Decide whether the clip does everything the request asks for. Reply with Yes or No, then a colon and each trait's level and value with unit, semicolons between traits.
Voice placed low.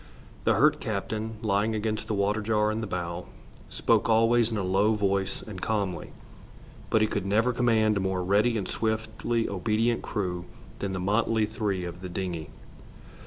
Yes: low, 105 Hz